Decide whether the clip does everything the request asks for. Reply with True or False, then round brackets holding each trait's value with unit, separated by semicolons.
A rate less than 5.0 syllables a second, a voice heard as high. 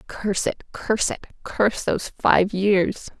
True (4.5 syllables/s; 200 Hz)